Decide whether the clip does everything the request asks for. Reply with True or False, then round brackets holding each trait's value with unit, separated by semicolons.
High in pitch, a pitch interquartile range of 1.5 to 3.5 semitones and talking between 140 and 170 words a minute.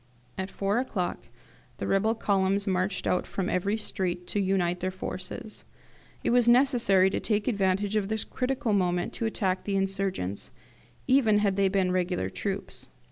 True (195 Hz; 2.6 semitones; 160 wpm)